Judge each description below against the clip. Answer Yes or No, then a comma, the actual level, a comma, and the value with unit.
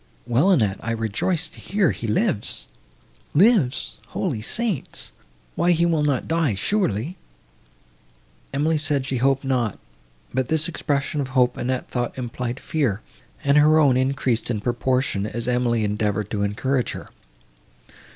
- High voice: No, low, 130 Hz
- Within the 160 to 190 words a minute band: No, average, 140 wpm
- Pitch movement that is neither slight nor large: Yes, average, 4.7 semitones